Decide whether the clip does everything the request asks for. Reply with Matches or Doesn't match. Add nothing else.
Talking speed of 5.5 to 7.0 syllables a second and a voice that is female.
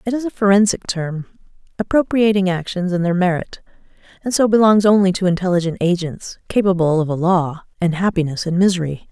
Matches